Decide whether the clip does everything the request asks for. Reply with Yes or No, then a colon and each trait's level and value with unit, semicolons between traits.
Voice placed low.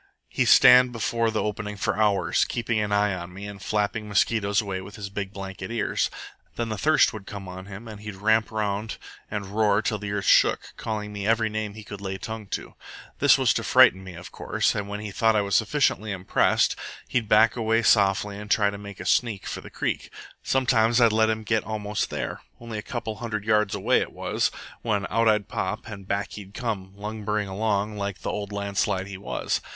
Yes: low, 105 Hz